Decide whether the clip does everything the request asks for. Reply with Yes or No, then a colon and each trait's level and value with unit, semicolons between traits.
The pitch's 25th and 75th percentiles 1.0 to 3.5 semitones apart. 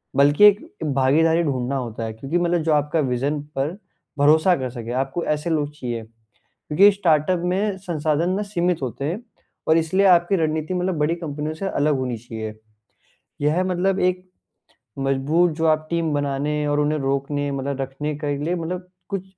No: average, 4.0 semitones